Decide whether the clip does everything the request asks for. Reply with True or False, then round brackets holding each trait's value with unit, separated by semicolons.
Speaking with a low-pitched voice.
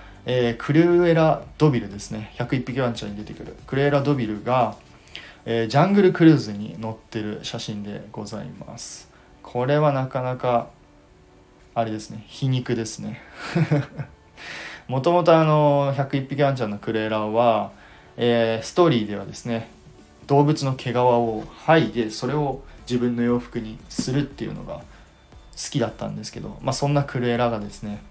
True (120 Hz)